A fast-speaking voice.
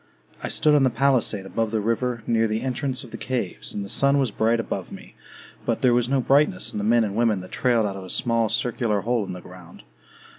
Yes: fast, 245 wpm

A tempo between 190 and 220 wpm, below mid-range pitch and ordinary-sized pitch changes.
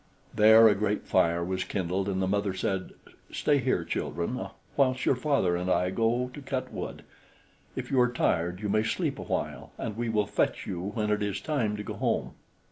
Yes: fast, 205 wpm; low, 105 Hz; average, 4.1 semitones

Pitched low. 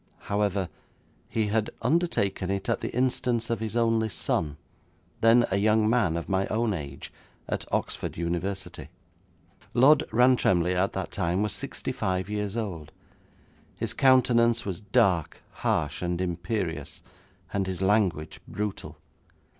Yes: low, 100 Hz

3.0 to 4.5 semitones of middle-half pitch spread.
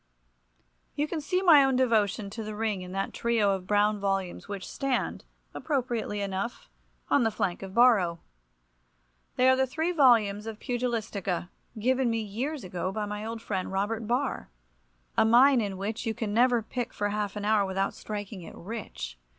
Yes: average, 3.7 semitones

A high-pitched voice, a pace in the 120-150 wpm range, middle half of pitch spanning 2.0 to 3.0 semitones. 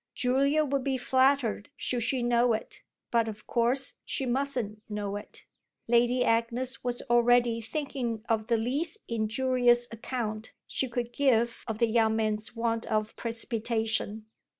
Yes: high, 235 Hz; average, 145 wpm; narrow, 2.4 semitones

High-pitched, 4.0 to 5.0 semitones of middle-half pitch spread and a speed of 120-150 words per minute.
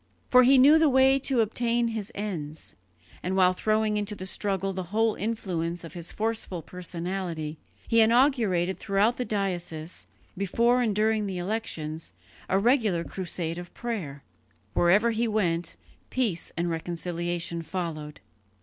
Yes: high, 195 Hz; average, 4.7 semitones; average, 140 wpm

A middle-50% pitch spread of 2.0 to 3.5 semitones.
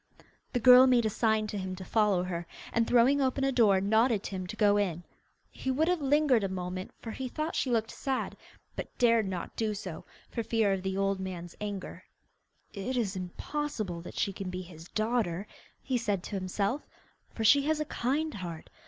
No: average, 4.9 semitones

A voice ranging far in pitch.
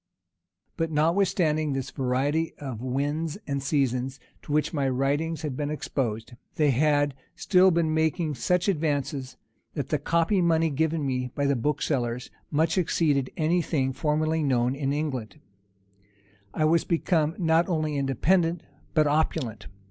No: average, 3.2 semitones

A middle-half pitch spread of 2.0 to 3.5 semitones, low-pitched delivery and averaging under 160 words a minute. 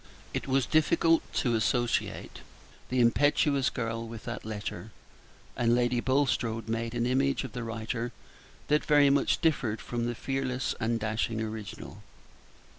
Yes: average, 2.9 semitones; low, 120 Hz; average, 140 wpm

